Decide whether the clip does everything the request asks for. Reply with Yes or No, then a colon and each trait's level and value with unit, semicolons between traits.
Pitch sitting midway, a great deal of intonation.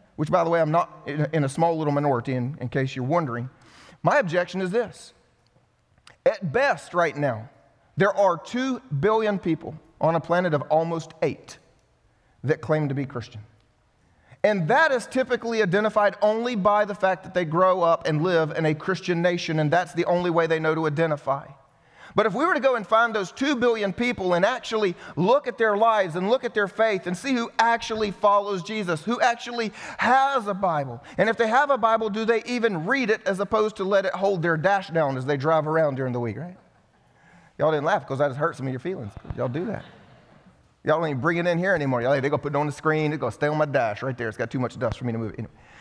Yes: medium, 175 Hz; wide, 6.4 semitones